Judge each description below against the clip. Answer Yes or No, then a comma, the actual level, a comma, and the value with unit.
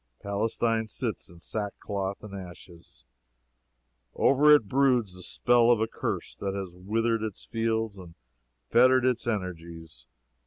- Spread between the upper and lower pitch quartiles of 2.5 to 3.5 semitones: No, average, 4.1 semitones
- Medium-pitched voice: No, low, 105 Hz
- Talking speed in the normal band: No, slow, 130 wpm